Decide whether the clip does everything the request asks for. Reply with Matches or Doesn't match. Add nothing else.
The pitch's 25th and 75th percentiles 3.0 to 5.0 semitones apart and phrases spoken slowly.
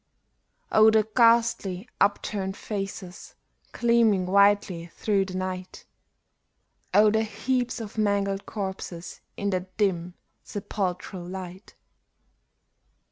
Doesn't match